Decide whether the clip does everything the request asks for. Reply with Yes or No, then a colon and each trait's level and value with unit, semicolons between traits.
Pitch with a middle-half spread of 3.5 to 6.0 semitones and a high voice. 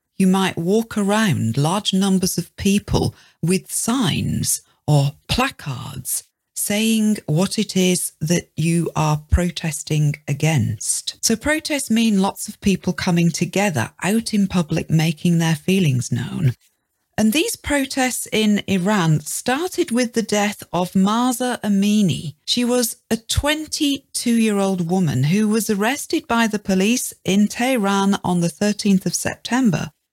Yes: average, 5.1 semitones; high, 195 Hz